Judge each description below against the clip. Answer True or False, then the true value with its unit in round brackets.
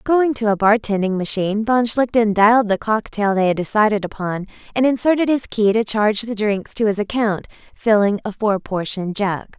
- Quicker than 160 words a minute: True (190 wpm)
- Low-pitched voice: False (215 Hz)